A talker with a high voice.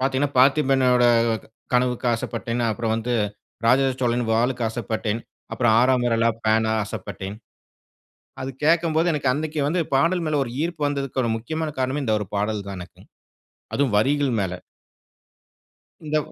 No: low, 125 Hz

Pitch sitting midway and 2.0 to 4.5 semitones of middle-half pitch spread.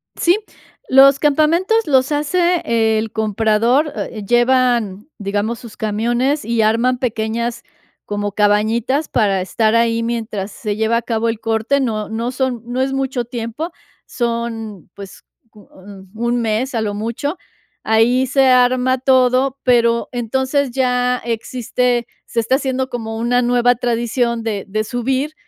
No: high, 235 Hz; average, 2.8 semitones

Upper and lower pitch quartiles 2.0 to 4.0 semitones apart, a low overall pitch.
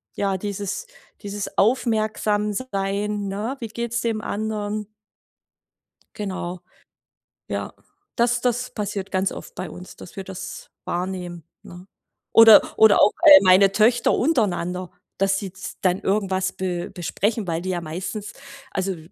No: narrow, 2.5 semitones; high, 200 Hz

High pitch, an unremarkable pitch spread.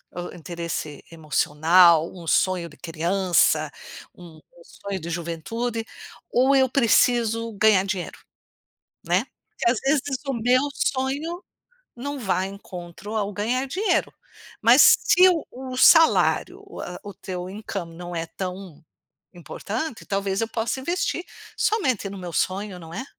No: high, 200 Hz; wide, 6.6 semitones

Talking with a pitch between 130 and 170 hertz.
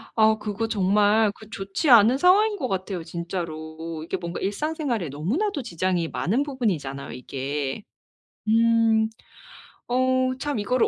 No: high, 210 Hz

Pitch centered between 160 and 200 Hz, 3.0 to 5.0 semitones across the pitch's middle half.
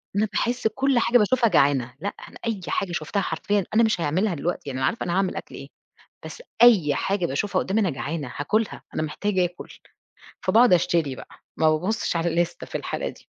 No: medium, 185 Hz; wide, 5.6 semitones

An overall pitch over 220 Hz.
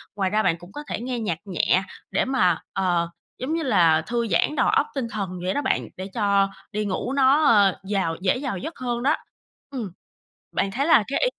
No: high, 210 Hz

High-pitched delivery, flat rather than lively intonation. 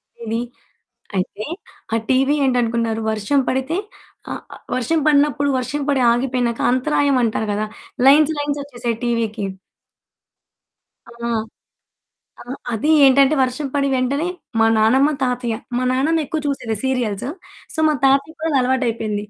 No: very high, 255 Hz; average, 3.5 semitones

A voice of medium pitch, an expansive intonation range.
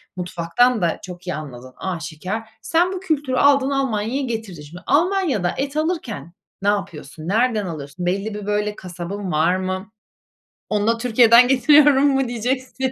No: high, 210 Hz; wide, 6.7 semitones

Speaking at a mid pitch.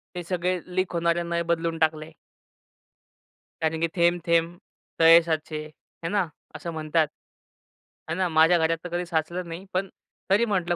Yes: medium, 170 Hz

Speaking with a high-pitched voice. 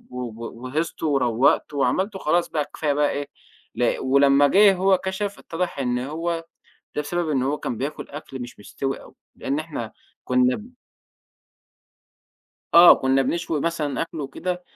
No: medium, 145 Hz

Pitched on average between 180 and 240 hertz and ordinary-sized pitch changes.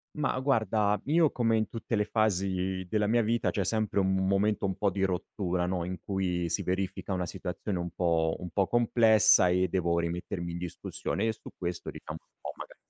No: very low, 95 Hz; average, 3.4 semitones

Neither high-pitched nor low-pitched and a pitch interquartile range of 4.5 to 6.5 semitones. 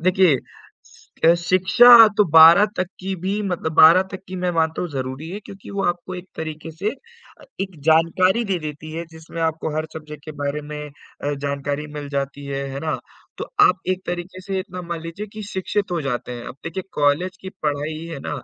No: medium, 165 Hz; average, 3.7 semitones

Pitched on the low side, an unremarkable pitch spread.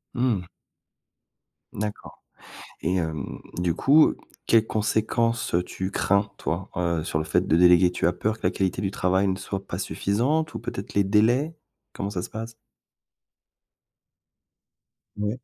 Yes: low, 100 Hz; average, 3.8 semitones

